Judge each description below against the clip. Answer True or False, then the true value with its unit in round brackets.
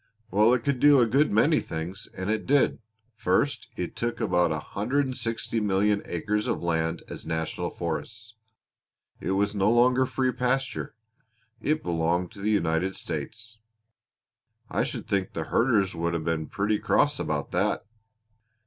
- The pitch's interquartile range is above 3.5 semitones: True (5.2 semitones)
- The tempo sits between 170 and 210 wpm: False (150 wpm)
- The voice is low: True (105 Hz)